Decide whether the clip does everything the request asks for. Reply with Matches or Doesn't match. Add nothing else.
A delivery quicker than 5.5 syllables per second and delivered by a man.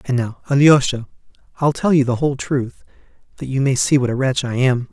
Matches